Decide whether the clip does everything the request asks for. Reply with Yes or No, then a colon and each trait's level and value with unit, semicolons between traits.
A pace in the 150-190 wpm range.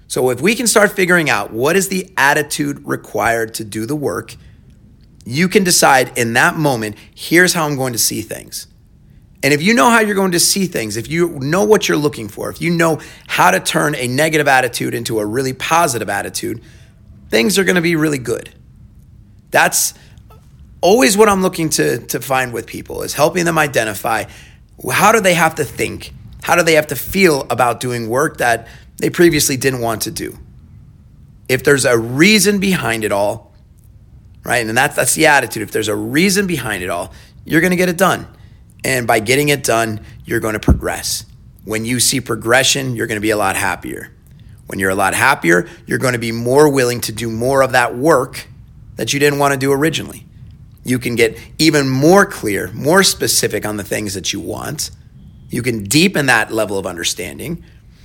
No: average, 200 wpm